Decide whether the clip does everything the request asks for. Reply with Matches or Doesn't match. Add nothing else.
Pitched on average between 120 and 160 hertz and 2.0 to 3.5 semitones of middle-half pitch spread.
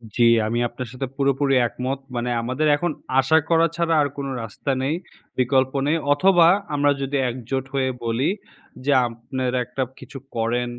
Matches